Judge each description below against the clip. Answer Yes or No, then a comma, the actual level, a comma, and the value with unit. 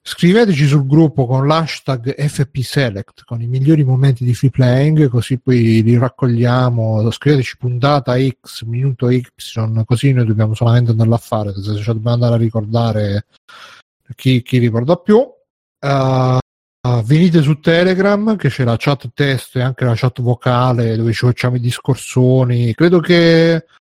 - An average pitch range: Yes, average, 3.3 semitones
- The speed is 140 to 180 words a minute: Yes, average, 155 wpm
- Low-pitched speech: Yes, low, 125 Hz